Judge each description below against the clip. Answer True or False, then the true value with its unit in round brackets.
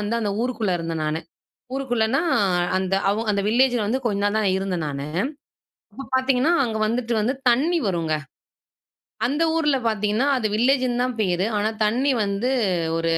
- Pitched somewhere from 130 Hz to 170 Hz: False (220 Hz)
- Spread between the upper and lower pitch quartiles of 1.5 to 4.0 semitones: False (4.5 semitones)